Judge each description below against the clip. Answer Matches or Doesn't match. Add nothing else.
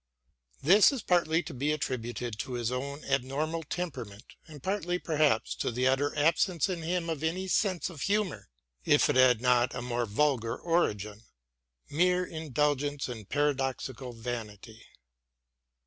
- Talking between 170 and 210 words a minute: Doesn't match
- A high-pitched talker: Doesn't match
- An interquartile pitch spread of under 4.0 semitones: Doesn't match